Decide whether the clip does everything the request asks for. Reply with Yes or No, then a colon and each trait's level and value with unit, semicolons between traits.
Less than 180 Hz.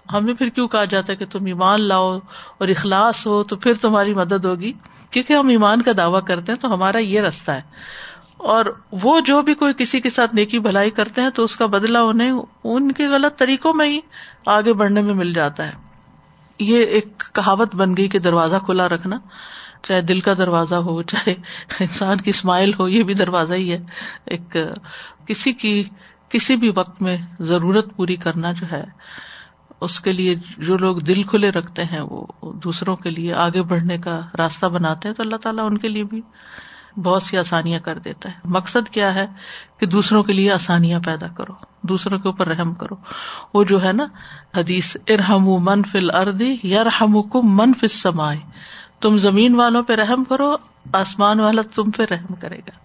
No: high, 200 Hz